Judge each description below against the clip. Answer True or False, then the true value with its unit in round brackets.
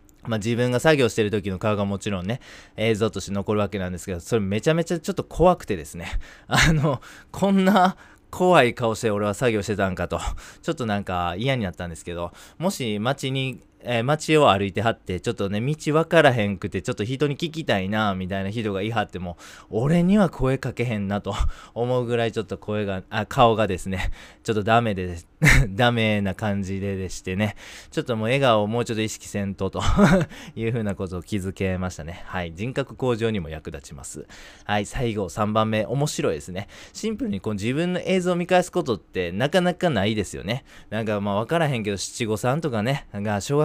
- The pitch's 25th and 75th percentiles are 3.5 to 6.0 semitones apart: True (5.4 semitones)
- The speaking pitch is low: True (110 Hz)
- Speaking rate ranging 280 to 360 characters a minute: False (405 characters per minute)